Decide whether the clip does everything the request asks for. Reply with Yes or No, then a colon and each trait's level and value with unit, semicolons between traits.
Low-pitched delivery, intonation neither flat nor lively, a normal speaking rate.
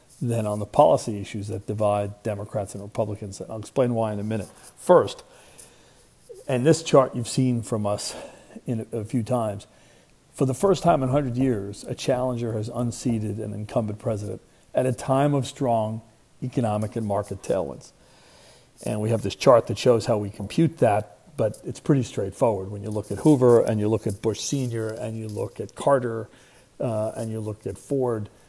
Yes: low, 115 Hz; average, 3.2 semitones; average, 190 wpm